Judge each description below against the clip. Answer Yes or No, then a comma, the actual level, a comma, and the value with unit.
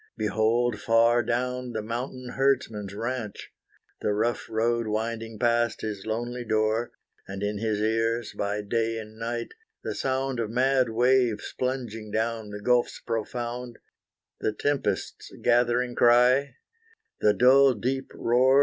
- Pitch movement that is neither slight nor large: No, narrow, 2.2 semitones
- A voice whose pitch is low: Yes, low, 115 Hz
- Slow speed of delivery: Yes, slow, 130 wpm